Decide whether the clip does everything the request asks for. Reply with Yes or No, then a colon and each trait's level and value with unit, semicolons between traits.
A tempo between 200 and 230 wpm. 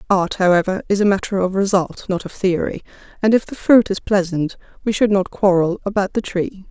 Yes: fast, 205 wpm